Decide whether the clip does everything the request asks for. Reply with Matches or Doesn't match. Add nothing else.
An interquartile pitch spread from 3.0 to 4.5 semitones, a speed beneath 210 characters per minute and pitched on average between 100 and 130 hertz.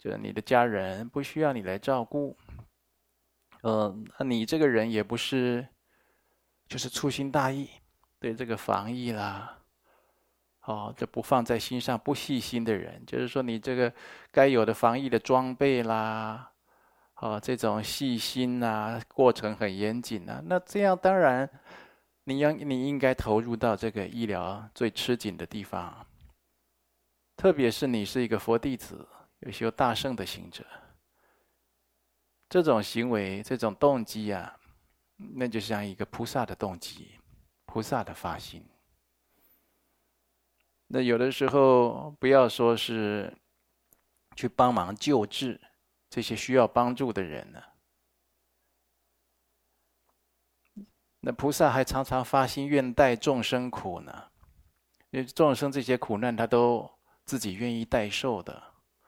Matches